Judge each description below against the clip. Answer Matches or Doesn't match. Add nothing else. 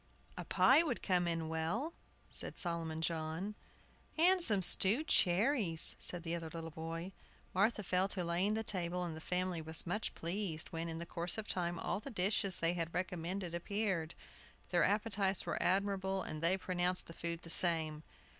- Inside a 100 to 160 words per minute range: Doesn't match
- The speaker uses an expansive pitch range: Doesn't match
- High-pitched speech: Doesn't match